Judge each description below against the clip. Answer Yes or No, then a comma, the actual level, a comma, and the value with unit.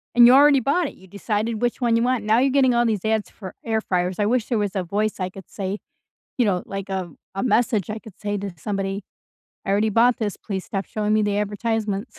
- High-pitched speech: Yes, high, 210 Hz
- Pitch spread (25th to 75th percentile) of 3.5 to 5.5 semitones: No, average, 3.0 semitones